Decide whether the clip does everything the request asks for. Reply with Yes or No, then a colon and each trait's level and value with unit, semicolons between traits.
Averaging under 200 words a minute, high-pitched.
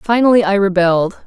Yes: average, 140 wpm; high, 200 Hz